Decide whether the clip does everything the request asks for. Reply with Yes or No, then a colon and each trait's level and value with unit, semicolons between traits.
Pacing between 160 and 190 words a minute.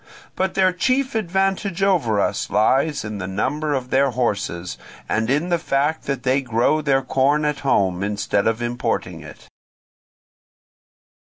No: average, 145 wpm